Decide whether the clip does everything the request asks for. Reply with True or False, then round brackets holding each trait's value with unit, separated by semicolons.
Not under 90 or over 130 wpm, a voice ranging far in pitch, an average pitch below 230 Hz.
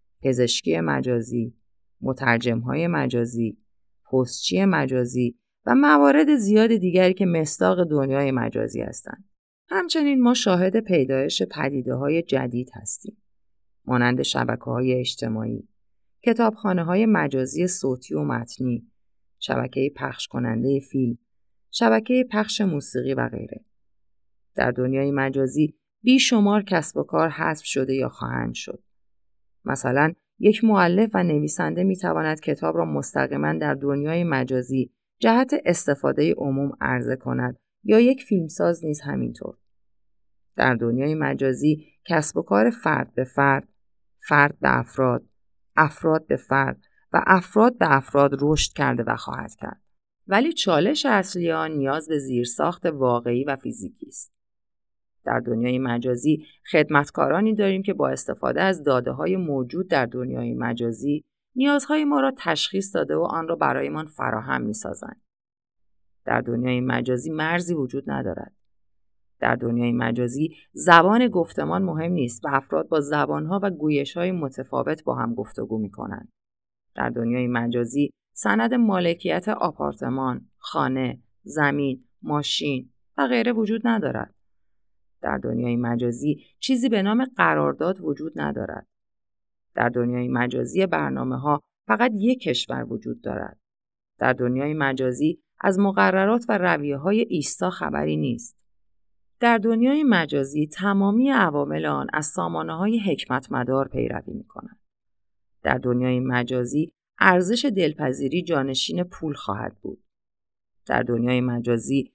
True (125 wpm; 6.8 semitones; 140 Hz)